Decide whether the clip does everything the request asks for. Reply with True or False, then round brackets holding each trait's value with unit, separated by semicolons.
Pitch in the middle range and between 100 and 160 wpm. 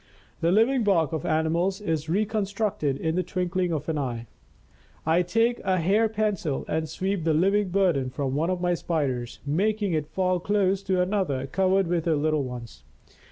False (175 Hz; 175 wpm)